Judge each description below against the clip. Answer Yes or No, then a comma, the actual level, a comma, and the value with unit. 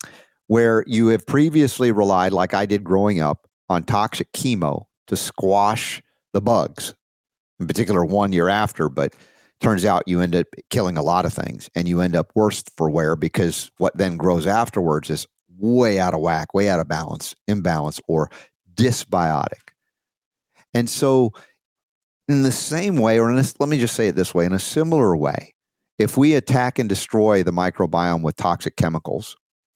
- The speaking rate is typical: Yes, average, 175 wpm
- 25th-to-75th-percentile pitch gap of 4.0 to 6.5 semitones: Yes, average, 5.2 semitones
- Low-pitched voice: Yes, low, 100 Hz